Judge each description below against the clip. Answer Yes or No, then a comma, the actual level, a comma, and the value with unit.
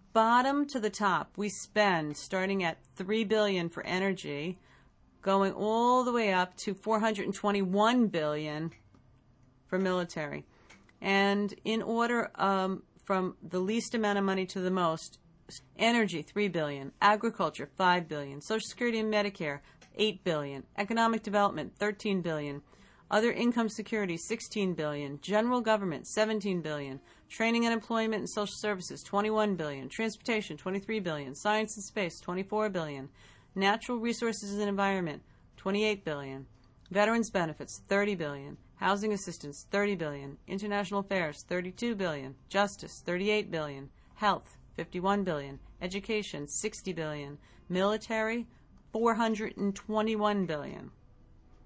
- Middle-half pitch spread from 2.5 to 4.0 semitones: No, average, 5.2 semitones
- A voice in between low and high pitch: No, high, 195 Hz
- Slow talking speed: Yes, slow, 130 wpm